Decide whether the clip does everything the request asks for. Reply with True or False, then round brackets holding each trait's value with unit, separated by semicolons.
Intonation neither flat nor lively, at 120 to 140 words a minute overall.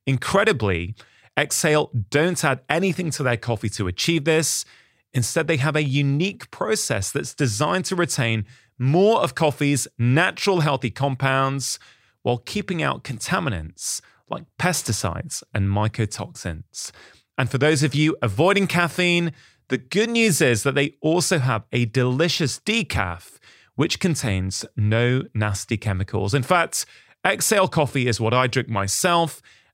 False (6.1 semitones; 135 wpm)